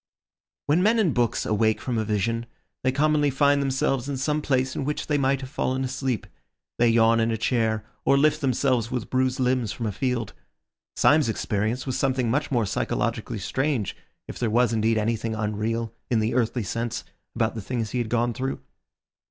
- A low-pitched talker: Yes, low, 120 Hz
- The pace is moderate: Yes, average, 190 wpm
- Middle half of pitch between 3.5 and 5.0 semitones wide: No, average, 3.0 semitones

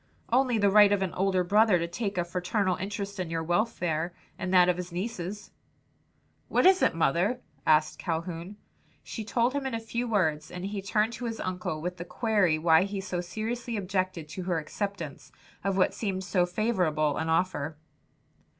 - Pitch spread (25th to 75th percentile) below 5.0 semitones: Yes, average, 3.6 semitones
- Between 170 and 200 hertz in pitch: Yes, medium, 185 Hz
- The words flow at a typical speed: Yes, average, 185 wpm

